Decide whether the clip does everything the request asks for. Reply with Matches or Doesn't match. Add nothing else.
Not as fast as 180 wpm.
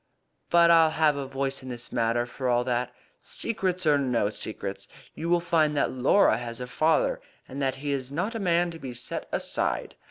Doesn't match